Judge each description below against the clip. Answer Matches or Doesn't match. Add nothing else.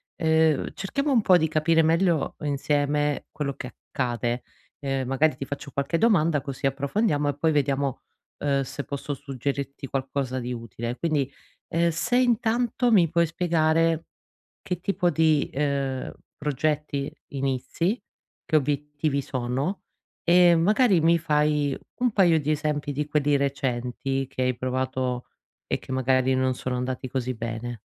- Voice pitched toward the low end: Doesn't match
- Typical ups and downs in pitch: Matches